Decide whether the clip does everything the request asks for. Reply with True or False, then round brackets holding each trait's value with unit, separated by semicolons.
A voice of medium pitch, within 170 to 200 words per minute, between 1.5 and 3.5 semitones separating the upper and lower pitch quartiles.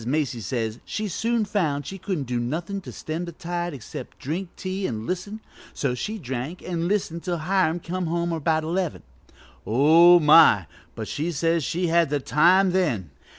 False (170 Hz; 180 wpm; 4.2 semitones)